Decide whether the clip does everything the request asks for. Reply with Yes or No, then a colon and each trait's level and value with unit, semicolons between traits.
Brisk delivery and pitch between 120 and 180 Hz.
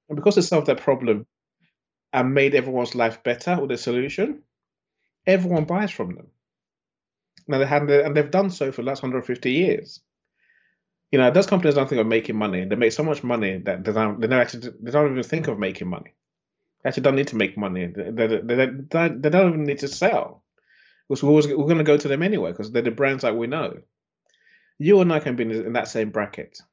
Yes: fast, 225 wpm; medium, 140 Hz